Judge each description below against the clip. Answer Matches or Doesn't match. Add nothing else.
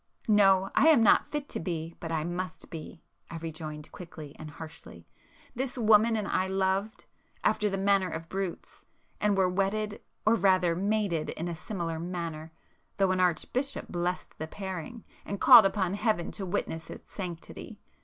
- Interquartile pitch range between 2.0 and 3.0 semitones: Doesn't match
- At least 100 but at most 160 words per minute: Matches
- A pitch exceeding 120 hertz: Matches